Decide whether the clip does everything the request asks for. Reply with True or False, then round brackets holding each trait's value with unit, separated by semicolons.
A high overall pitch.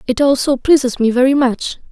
True (260 Hz)